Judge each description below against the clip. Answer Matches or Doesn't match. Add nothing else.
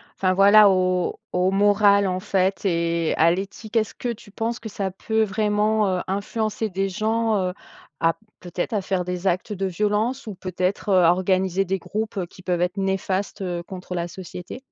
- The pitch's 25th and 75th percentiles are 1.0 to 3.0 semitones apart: Matches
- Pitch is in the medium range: Doesn't match